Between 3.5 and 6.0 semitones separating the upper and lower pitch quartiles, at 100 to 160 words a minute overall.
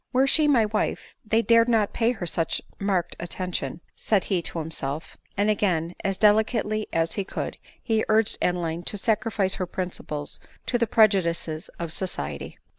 No: average, 4.5 semitones; average, 175 wpm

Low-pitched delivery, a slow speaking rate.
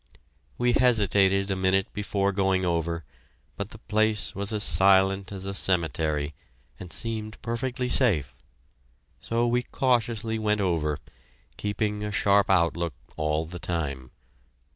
Yes: low, 100 Hz; slow, 130 wpm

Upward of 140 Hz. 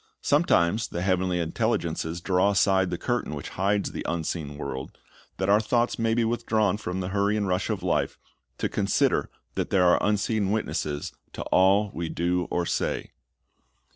No: very low, 95 Hz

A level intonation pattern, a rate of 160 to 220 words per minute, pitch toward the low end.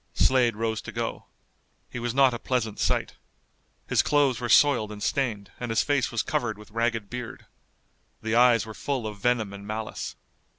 Yes: narrow, 2.3 semitones; average, 180 wpm; low, 115 Hz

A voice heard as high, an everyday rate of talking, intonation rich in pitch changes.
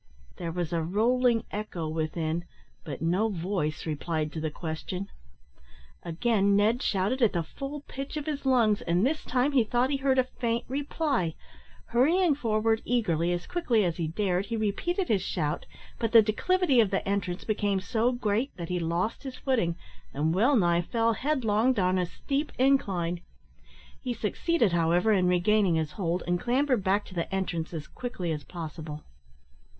Yes: high, 205 Hz; average, 170 wpm; wide, 6.3 semitones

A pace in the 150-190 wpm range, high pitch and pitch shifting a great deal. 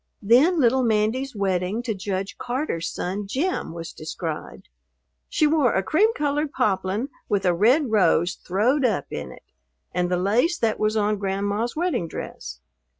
Yes: average, 155 wpm; high, 210 Hz; wide, 5.8 semitones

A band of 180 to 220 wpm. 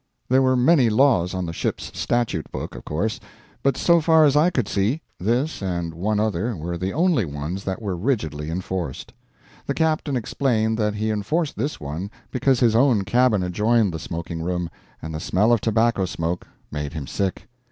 Yes: average, 185 wpm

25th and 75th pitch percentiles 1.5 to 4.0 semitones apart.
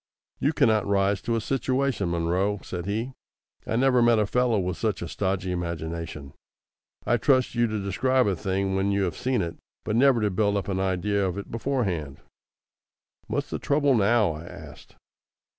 No: average, 4.4 semitones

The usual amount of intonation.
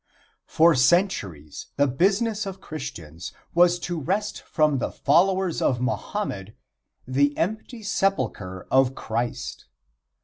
No: wide, 7.5 semitones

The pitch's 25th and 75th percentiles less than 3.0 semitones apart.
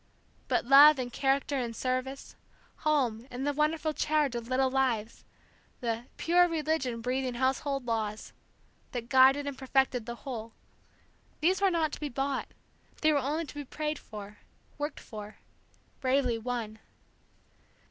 No: average, 3.5 semitones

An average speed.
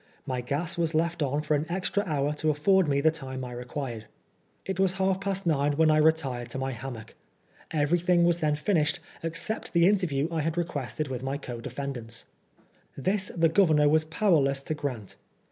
Yes: average, 185 wpm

